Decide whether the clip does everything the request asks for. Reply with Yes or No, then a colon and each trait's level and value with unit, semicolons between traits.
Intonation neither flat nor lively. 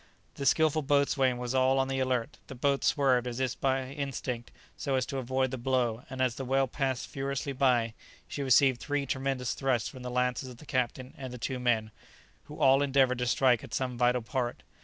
No: narrow, 1.6 semitones